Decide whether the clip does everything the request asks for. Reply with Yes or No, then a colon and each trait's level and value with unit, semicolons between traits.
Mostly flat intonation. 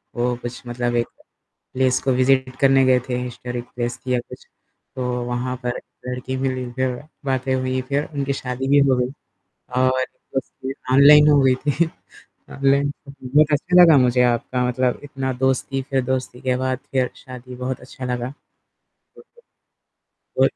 Yes: narrow, 1.4 semitones